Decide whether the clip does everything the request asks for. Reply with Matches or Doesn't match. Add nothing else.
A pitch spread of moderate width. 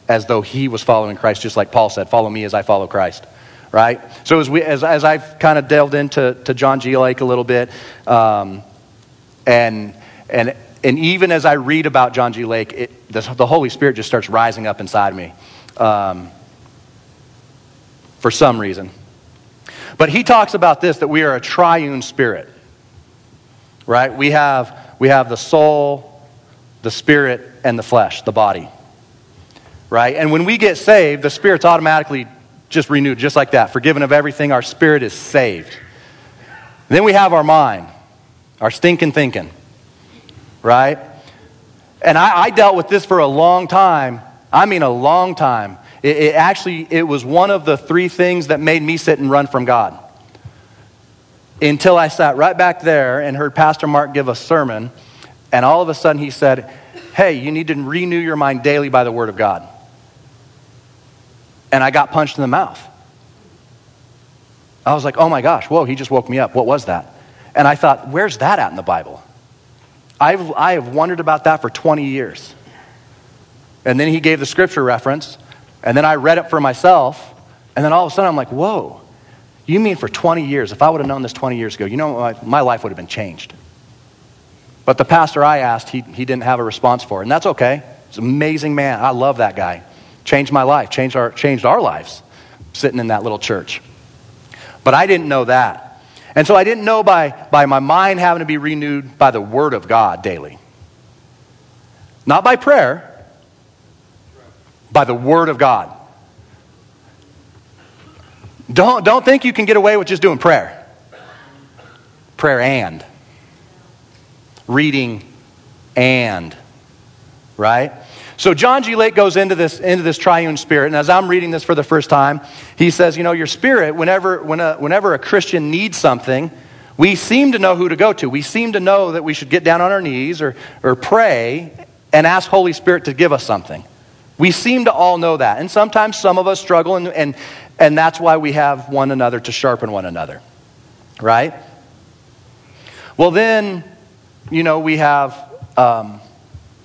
Matches